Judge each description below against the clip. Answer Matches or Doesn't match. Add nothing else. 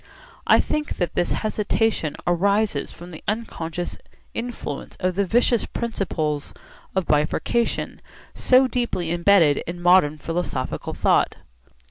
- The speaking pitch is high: Doesn't match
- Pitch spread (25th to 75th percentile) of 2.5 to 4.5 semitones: Doesn't match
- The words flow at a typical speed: Doesn't match